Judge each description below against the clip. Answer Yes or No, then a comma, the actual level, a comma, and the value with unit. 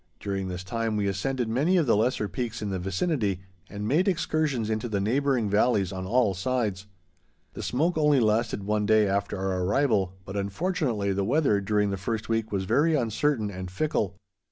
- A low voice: Yes, low, 110 Hz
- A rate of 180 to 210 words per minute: Yes, average, 185 wpm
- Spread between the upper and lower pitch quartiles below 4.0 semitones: No, average, 4.7 semitones